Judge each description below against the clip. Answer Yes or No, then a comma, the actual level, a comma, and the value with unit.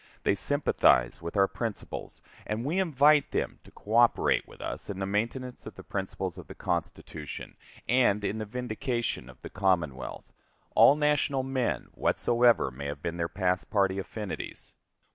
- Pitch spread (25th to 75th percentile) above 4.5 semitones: Yes, wide, 5.5 semitones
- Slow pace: No, average, 160 wpm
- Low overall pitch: Yes, low, 105 Hz